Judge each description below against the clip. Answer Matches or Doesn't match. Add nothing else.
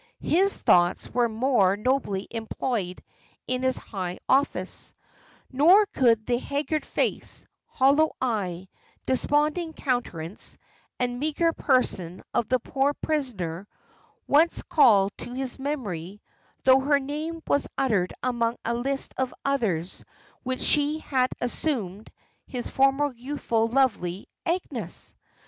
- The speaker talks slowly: Matches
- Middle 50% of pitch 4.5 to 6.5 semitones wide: Matches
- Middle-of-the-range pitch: Doesn't match